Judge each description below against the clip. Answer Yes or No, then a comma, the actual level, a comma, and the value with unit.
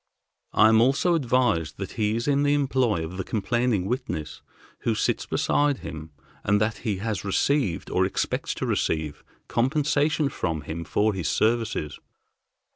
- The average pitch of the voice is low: Yes, low, 110 Hz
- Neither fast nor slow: Yes, average, 155 wpm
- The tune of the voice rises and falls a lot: Yes, wide, 6.4 semitones